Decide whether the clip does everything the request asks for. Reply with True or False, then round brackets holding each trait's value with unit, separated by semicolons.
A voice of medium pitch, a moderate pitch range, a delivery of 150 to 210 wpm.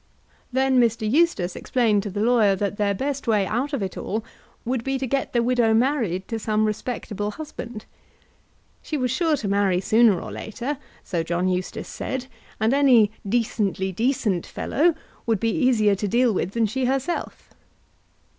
False (225 Hz; 4.1 semitones; 170 wpm)